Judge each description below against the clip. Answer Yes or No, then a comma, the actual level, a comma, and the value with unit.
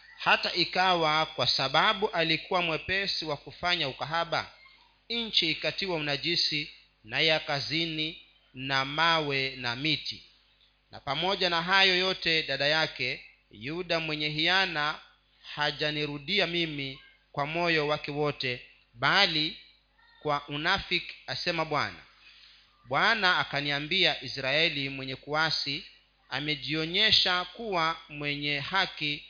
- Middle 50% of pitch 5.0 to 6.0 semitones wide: No, average, 3.7 semitones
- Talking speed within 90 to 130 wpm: Yes, slow, 100 wpm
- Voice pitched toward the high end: No, medium, 155 Hz